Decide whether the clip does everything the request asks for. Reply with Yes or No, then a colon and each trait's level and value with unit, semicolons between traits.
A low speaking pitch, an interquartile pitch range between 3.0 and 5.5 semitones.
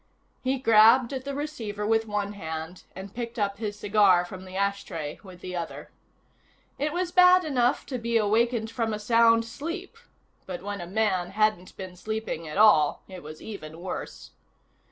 No: high, 210 Hz; average, 4.0 semitones